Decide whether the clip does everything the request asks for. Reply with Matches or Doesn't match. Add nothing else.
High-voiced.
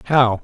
Doesn't match